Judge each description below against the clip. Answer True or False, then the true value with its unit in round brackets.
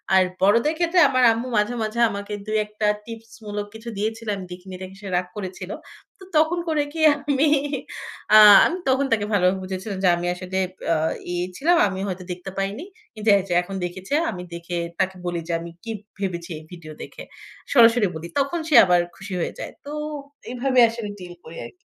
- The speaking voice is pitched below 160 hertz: False (205 Hz)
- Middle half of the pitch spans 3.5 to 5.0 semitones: True (4.4 semitones)